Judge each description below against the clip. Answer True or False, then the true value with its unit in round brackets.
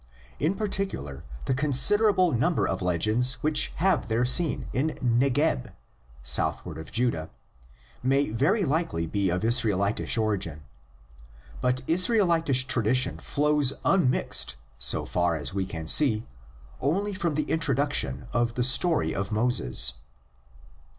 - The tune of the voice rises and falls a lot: True (7.5 semitones)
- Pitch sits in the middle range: False (125 Hz)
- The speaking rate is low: True (130 wpm)